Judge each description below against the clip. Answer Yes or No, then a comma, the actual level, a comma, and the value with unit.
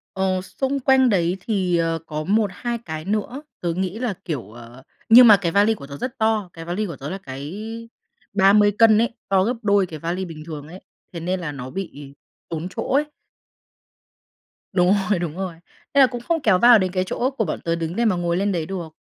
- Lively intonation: No, average, 4.6 semitones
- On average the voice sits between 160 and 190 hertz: Yes, medium, 185 Hz